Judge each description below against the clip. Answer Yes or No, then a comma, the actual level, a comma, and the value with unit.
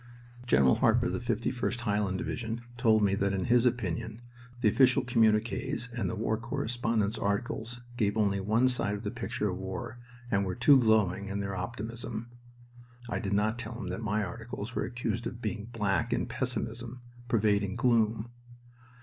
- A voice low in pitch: Yes, low, 110 Hz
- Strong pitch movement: No, average, 2.7 semitones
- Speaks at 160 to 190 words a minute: Yes, average, 170 wpm